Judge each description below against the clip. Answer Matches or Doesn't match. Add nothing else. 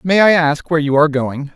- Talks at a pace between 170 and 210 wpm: Doesn't match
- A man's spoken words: Matches